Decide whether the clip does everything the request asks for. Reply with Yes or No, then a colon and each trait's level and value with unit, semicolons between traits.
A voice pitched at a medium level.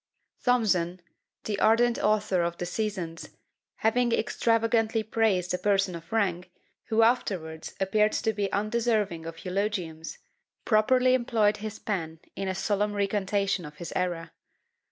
No: high, 205 Hz